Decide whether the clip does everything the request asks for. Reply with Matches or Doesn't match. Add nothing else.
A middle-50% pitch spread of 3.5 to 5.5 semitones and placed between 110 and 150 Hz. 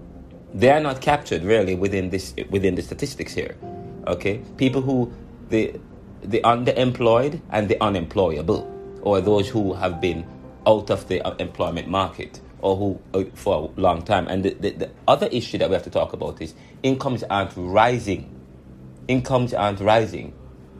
Doesn't match